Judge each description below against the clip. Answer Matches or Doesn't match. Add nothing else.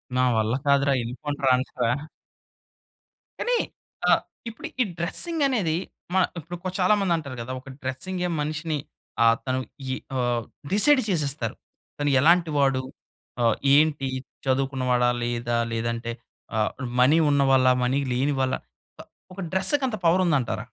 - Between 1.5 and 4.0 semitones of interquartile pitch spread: Doesn't match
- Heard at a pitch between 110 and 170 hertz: Matches